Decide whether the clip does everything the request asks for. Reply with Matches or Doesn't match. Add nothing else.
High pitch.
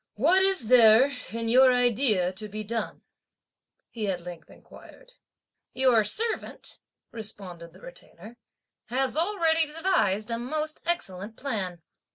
Matches